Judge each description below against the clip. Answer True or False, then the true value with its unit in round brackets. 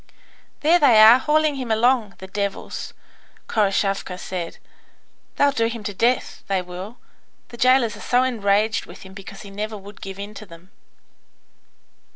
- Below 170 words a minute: True (160 wpm)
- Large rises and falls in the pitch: False (3.8 semitones)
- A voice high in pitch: True (215 Hz)